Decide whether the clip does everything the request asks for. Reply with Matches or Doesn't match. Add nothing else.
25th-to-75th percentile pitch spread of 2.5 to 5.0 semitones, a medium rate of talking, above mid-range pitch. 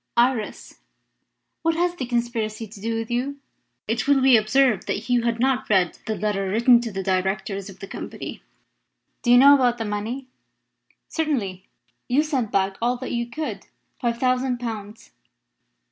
Matches